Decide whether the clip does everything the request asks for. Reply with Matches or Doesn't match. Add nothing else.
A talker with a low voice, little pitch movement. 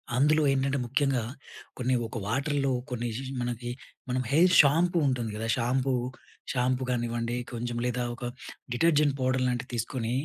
Matches